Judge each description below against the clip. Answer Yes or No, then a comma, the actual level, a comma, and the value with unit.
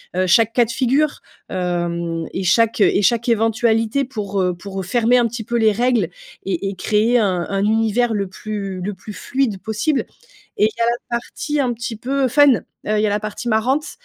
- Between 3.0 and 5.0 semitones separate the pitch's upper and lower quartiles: Yes, average, 3.4 semitones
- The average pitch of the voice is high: Yes, high, 220 Hz